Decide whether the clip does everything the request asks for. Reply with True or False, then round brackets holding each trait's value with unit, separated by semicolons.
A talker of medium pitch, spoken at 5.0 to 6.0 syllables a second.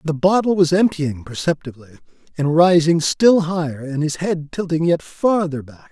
False (160 Hz; 4.8 syllables/s)